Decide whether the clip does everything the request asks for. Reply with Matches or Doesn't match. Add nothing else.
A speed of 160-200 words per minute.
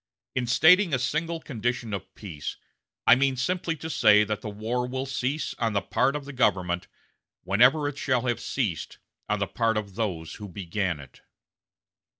Matches